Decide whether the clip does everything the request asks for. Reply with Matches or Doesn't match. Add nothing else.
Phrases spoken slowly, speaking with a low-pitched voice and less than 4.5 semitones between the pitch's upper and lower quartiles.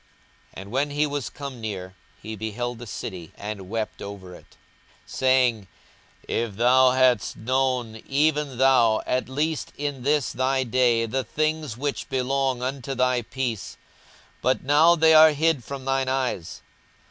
Doesn't match